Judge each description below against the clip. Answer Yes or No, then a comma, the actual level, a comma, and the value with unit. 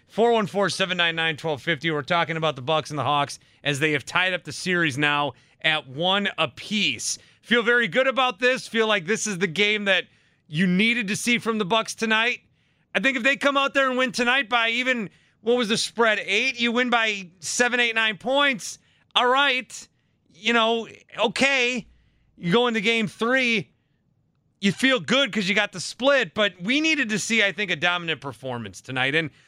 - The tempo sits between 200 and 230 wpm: Yes, fast, 205 wpm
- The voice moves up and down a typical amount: No, wide, 6.7 semitones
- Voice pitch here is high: Yes, high, 210 Hz